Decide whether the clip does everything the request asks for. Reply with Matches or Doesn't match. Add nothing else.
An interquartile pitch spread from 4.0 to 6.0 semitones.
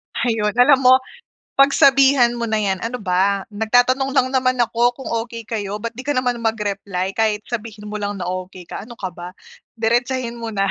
Doesn't match